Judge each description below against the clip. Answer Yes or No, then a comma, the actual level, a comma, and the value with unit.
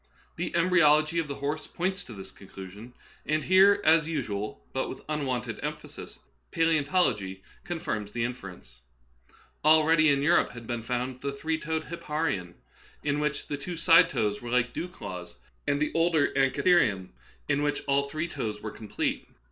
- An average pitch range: No, wide, 5.8 semitones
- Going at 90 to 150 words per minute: No, average, 165 wpm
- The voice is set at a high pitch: No, medium, 140 Hz